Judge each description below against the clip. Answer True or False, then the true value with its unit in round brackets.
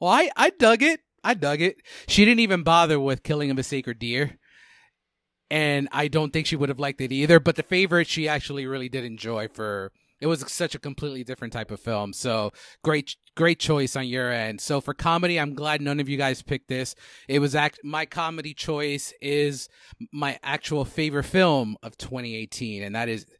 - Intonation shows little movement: False (3.4 semitones)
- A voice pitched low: False (145 Hz)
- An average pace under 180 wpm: False (205 wpm)